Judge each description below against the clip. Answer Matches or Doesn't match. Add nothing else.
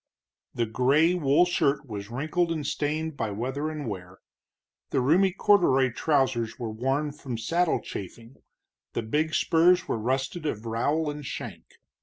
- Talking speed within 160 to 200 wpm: Doesn't match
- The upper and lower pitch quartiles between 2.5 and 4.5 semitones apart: Doesn't match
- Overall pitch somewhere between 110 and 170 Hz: Matches